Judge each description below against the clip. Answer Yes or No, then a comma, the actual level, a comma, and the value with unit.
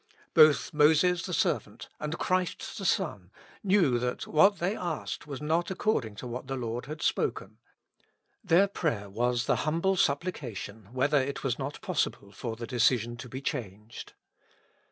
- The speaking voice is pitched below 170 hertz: Yes, medium, 140 Hz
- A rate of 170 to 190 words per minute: No, average, 160 wpm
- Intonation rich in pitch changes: Yes, wide, 6.0 semitones